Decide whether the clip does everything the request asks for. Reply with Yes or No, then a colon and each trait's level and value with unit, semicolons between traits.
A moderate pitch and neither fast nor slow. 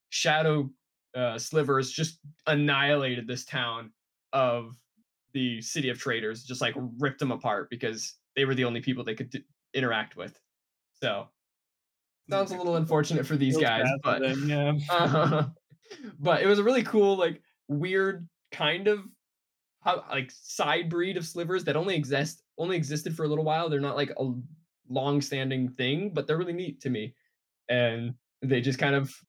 Yes: medium, 145 Hz; average, 170 wpm